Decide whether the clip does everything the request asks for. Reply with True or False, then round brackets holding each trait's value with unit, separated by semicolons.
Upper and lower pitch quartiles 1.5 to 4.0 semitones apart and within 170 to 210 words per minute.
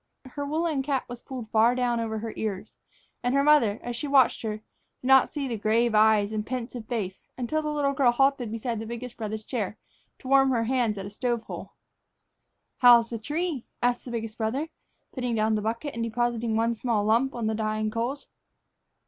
True (3.2 semitones; 200 wpm)